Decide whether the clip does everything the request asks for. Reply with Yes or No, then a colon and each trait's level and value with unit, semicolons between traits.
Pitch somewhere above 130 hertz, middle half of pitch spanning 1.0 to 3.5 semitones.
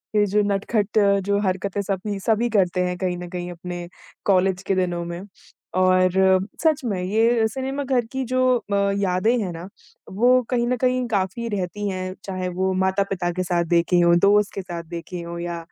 Yes: high, 190 Hz; average, 2.9 semitones